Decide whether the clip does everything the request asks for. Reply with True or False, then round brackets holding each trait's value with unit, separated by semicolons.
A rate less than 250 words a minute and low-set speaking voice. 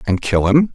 True (240 wpm; 120 Hz)